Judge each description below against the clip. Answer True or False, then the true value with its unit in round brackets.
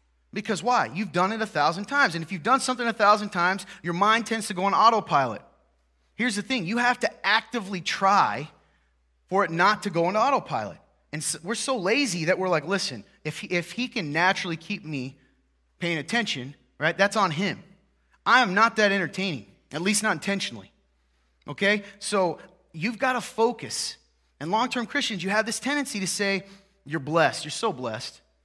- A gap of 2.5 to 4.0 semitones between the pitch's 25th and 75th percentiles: False (5.3 semitones)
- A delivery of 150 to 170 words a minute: False (190 wpm)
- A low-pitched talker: False (195 Hz)